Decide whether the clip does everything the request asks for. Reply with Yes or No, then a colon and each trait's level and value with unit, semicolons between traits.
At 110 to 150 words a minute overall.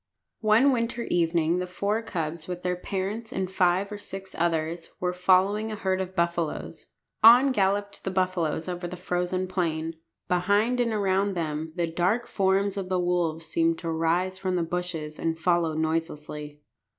No: average, 165 wpm